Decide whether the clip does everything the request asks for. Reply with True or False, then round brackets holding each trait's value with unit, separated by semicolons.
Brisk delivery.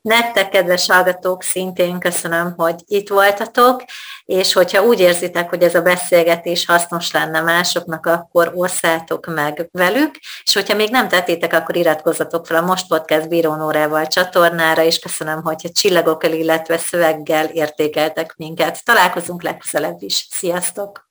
False (140 wpm)